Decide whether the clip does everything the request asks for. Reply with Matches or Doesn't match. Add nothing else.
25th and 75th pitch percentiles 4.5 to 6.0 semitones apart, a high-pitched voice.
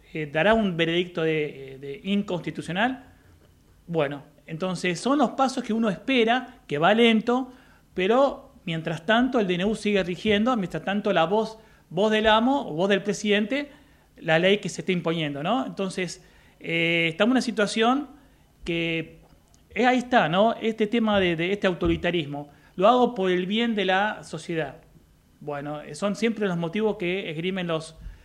Matches